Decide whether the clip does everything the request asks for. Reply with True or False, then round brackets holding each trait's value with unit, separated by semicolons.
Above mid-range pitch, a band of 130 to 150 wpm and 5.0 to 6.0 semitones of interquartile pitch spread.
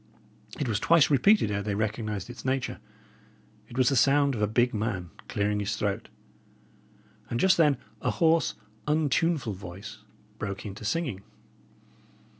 False (115 Hz; 145 wpm; 5.5 semitones)